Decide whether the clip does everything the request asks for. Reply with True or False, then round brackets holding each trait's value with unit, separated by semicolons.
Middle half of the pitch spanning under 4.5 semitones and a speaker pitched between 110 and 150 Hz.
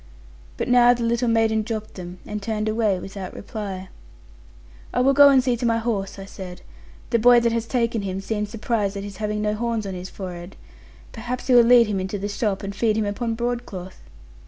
False (3.1 semitones; 215 Hz)